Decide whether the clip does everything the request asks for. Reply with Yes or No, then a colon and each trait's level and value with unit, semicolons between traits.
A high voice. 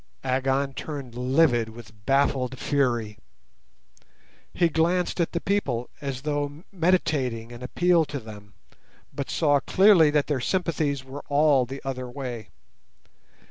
No: medium, 140 Hz